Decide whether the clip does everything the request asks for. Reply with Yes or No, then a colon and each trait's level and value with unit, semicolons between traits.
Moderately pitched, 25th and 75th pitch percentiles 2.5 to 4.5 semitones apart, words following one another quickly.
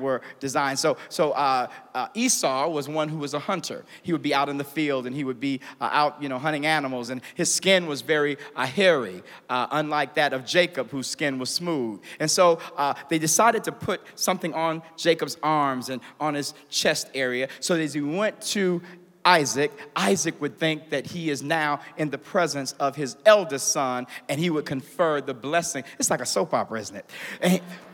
Yes: medium, 150 Hz; average, 3.5 semitones; fast, 210 wpm